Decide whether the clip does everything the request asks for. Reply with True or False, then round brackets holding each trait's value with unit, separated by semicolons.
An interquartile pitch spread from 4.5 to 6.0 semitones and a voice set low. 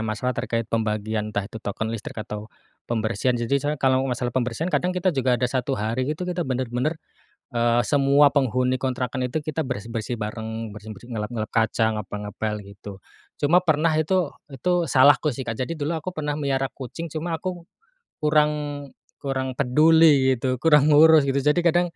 True (4.8 semitones; 130 Hz)